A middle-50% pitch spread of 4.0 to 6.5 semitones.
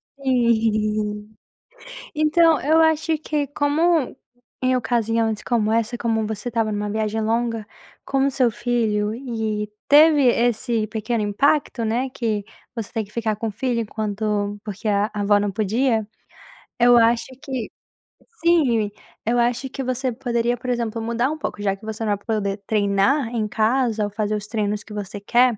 No: average, 3.0 semitones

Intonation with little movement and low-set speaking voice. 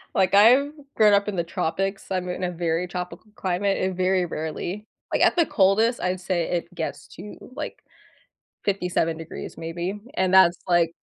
No: narrow, 2.3 semitones; medium, 185 Hz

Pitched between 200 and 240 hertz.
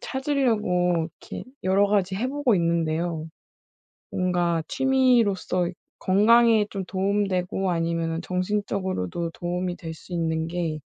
No: medium, 185 Hz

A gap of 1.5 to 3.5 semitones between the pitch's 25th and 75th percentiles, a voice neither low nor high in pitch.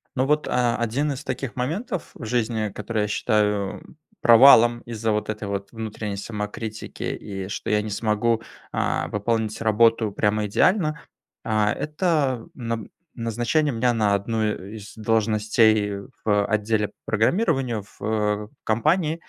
No: narrow, 2.6 semitones; low, 110 Hz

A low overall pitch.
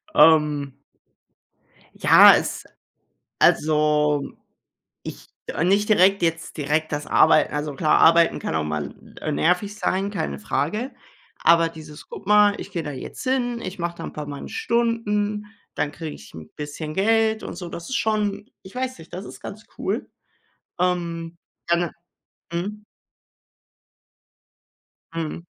No: medium, 170 Hz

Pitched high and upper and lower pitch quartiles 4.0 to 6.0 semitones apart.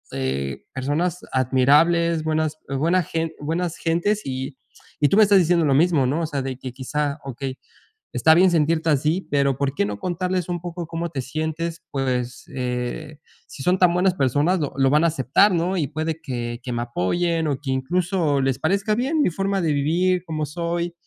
No: medium, 155 Hz; average, 4.3 semitones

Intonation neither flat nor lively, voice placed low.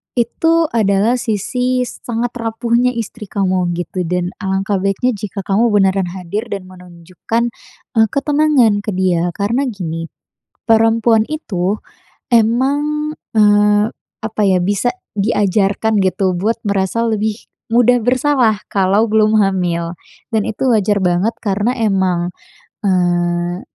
No: average, 3.7 semitones; high, 210 Hz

